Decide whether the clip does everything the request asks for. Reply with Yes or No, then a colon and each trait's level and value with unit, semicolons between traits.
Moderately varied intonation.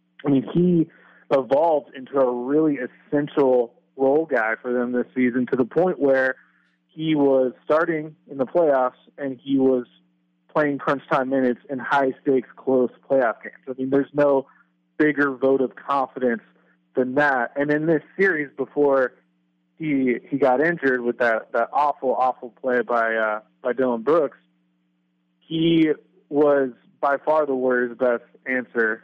Yes: average, 3.0 semitones